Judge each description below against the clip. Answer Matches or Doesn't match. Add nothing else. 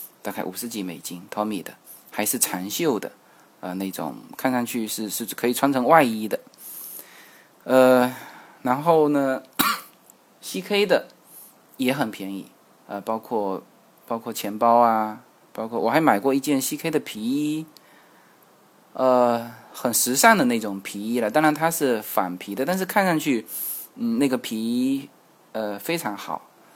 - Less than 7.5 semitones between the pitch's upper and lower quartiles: Matches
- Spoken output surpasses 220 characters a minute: Doesn't match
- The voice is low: Matches